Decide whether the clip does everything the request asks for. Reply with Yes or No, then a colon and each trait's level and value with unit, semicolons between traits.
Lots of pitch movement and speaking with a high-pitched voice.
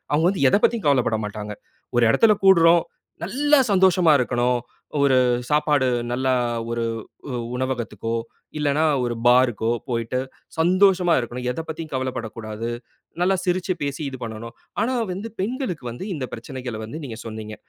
No: wide, 7.0 semitones; low, 130 Hz